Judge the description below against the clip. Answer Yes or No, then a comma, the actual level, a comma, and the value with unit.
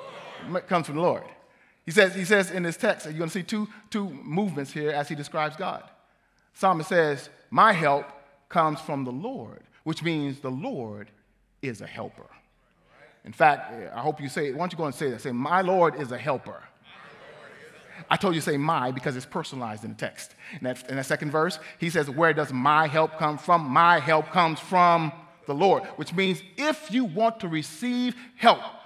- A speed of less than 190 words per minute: No, average, 200 wpm